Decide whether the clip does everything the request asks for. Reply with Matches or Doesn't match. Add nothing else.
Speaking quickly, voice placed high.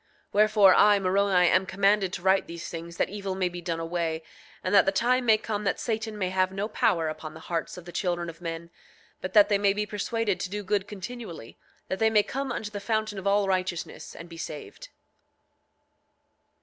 Matches